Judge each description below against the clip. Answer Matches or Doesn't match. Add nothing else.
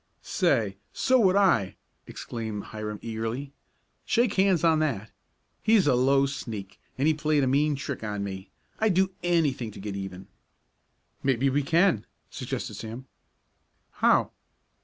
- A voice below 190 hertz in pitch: Matches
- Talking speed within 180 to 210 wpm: Doesn't match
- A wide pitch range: Matches